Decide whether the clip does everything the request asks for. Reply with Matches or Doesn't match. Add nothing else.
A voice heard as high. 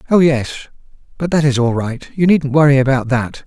Doesn't match